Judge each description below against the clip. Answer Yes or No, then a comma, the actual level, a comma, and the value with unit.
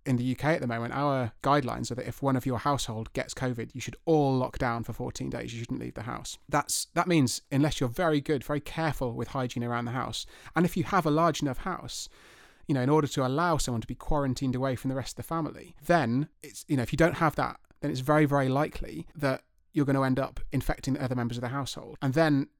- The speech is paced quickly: Yes, fast, 260 wpm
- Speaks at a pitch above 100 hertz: Yes, low, 135 Hz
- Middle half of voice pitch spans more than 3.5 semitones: No, average, 3.2 semitones